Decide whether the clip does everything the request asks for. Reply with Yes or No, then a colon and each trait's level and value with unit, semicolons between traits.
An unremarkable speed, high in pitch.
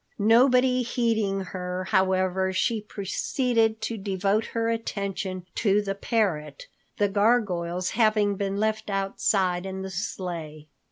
No: slow, 120 wpm; high, 200 Hz